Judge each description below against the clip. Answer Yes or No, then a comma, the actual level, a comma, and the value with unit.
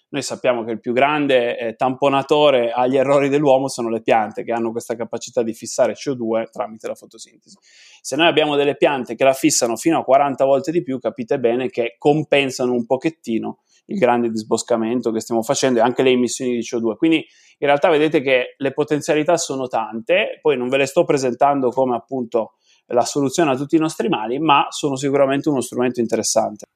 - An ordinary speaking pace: No, fast, 190 wpm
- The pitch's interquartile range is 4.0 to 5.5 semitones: No, average, 3.3 semitones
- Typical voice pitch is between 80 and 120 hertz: No, low, 135 Hz